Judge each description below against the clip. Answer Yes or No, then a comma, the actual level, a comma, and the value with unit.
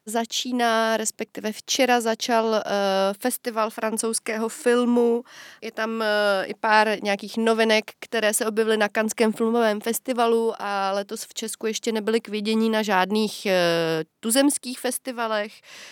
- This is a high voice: Yes, high, 220 Hz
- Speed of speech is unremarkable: Yes, average, 130 wpm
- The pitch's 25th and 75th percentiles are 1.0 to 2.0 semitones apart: Yes, narrow, 1.5 semitones